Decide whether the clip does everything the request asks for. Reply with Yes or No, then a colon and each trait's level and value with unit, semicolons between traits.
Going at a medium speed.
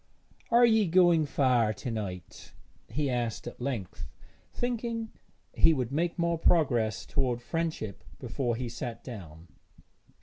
No: slow, 130 wpm